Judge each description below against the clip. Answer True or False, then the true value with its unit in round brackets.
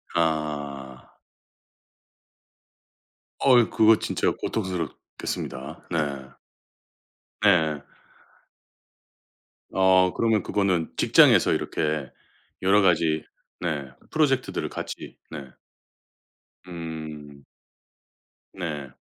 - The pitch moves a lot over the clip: False (4.4 semitones)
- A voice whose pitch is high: False (80 Hz)